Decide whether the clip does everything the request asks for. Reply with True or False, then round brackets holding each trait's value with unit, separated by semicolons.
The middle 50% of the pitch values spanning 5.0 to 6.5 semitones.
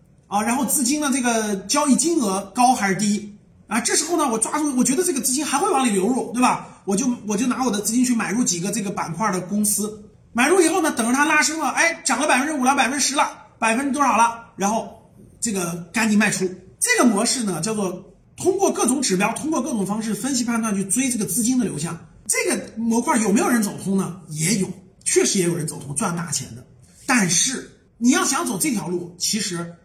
True (5.6 semitones)